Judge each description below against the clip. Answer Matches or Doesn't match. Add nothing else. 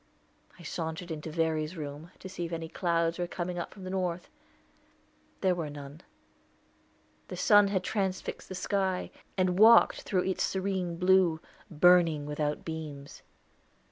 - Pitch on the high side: Doesn't match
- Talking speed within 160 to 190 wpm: Doesn't match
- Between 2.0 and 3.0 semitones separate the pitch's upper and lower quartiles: Matches